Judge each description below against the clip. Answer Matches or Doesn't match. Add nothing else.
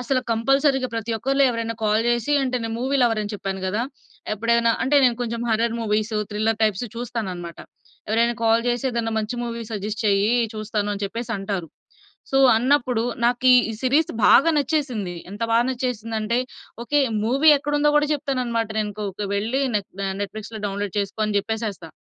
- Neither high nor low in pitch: Doesn't match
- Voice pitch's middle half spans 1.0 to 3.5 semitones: Matches